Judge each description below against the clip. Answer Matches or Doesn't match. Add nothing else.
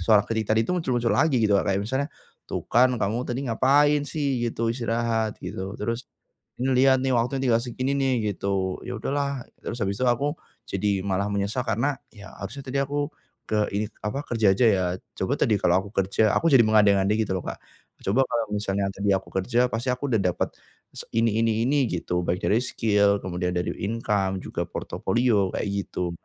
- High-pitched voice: Doesn't match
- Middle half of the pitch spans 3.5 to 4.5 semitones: Matches